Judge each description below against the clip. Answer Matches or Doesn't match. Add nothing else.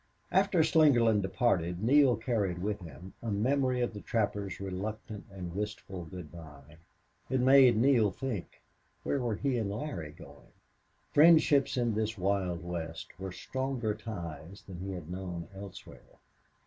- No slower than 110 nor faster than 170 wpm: Matches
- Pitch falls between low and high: Doesn't match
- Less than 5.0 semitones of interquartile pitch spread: Doesn't match